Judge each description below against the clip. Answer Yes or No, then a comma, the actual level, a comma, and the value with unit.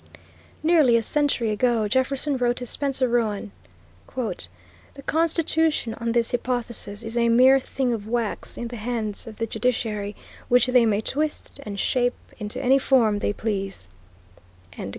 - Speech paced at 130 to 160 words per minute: Yes, average, 150 wpm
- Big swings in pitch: No, average, 3.1 semitones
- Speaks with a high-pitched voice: Yes, high, 240 Hz